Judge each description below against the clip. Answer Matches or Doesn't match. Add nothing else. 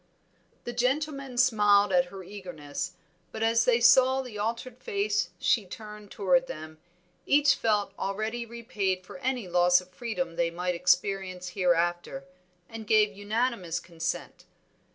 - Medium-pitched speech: Doesn't match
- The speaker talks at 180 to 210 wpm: Doesn't match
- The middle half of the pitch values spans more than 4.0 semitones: Matches